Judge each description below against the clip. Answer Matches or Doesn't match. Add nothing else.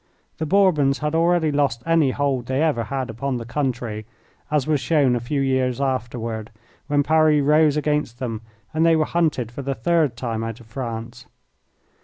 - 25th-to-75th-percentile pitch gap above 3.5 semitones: Matches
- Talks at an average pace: Matches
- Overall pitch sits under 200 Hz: Matches